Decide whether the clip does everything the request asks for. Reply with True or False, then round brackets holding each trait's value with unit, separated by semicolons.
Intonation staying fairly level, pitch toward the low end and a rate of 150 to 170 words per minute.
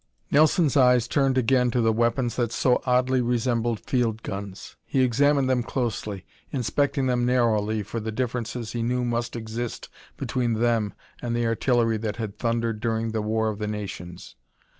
True (2.2 semitones; 120 Hz; 165 wpm)